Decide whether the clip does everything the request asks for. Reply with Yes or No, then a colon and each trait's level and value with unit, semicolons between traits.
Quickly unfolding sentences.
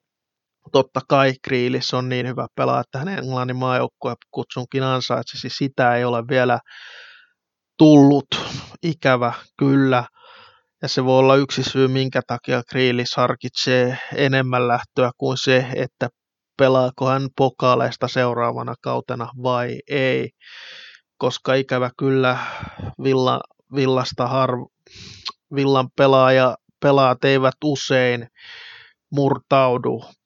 No: average, 110 wpm